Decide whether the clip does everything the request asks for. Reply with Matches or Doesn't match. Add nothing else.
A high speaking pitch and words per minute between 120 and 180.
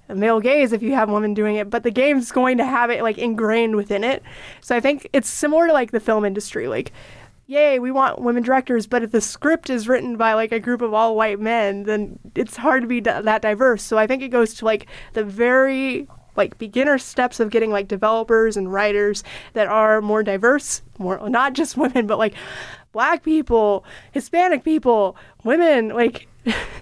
Doesn't match